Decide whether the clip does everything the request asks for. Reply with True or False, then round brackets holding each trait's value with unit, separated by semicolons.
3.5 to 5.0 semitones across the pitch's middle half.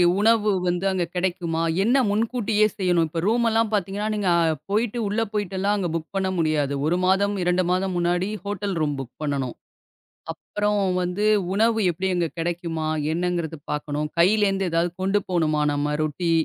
True (3.8 semitones)